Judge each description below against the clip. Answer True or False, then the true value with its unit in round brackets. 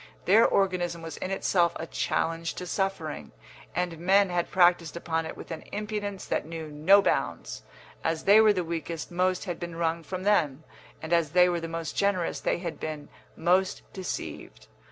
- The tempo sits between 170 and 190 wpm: True (180 wpm)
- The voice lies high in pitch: False (175 Hz)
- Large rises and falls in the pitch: False (2.4 semitones)